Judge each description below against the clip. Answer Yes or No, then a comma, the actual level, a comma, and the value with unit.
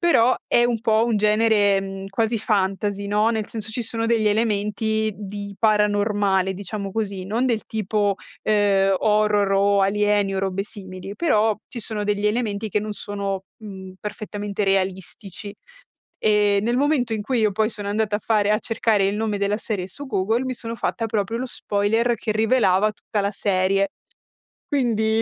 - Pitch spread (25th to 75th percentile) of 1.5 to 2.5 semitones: Yes, narrow, 1.8 semitones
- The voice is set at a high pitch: Yes, high, 210 Hz